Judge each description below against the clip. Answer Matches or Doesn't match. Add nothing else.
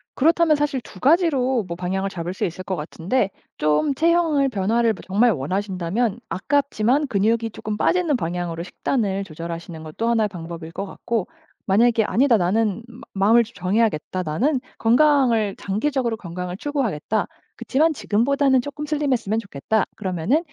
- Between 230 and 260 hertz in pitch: Doesn't match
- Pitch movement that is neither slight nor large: Doesn't match